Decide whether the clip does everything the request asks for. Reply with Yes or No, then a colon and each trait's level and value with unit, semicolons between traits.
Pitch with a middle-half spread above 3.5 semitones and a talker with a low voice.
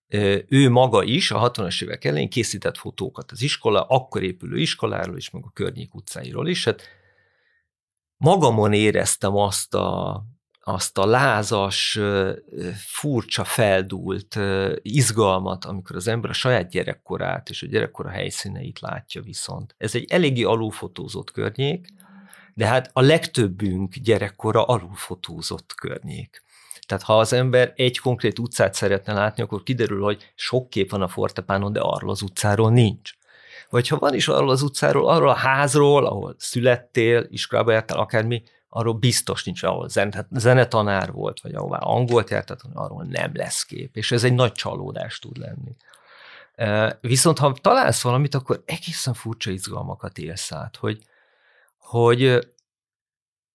Yes: average, 4.0 semitones; low, 115 Hz